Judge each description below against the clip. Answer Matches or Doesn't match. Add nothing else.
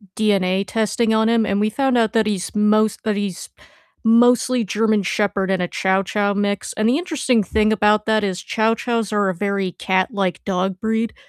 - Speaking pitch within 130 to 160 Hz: Doesn't match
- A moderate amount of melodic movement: Doesn't match